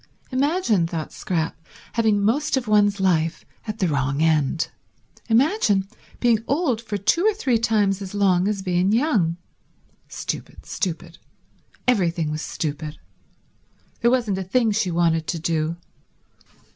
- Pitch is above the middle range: Yes, high, 195 Hz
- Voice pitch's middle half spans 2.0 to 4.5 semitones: No, wide, 5.5 semitones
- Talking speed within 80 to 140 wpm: Yes, slow, 135 wpm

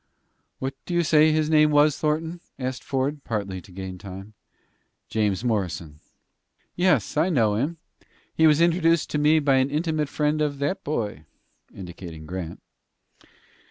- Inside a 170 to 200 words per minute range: No, average, 150 wpm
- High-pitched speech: No, medium, 140 Hz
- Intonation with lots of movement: Yes, wide, 7.5 semitones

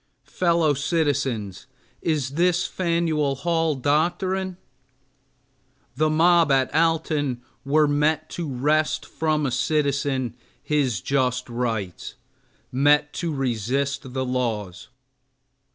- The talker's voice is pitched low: No, medium, 145 Hz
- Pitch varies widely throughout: No, average, 3.7 semitones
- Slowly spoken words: Yes, slow, 100 wpm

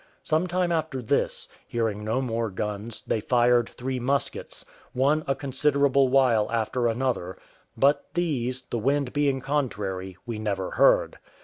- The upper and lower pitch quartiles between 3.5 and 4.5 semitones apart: Yes, average, 3.8 semitones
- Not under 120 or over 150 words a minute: Yes, average, 140 wpm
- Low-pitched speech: Yes, low, 125 Hz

